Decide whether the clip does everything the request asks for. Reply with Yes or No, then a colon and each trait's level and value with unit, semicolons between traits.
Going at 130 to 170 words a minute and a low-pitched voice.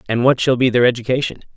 No: fast, 230 wpm; low, 125 Hz